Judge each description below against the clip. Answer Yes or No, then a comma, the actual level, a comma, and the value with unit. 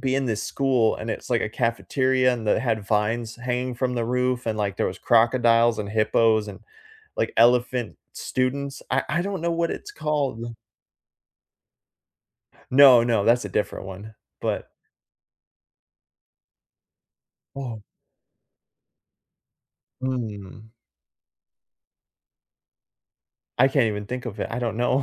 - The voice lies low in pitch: Yes, low, 120 Hz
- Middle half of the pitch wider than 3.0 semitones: No, average, 2.7 semitones